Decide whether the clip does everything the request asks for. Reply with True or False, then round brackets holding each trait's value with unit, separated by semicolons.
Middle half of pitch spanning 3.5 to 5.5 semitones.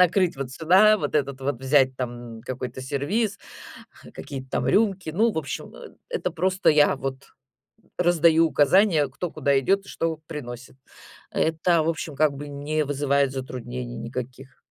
True (4.2 semitones)